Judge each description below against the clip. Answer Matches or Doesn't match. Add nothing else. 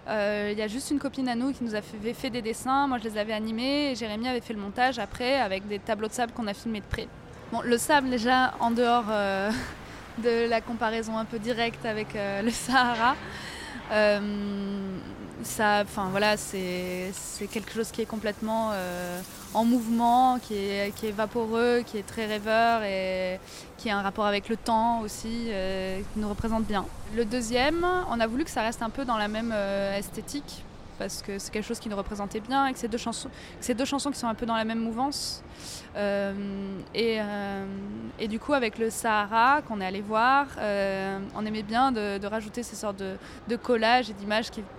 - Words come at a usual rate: Matches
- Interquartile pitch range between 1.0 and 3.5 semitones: Matches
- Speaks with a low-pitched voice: Doesn't match